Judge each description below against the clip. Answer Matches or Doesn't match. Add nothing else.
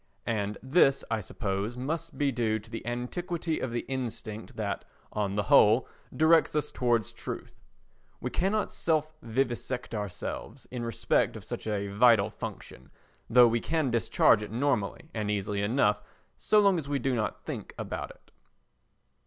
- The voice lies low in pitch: Matches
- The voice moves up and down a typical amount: Matches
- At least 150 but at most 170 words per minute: Matches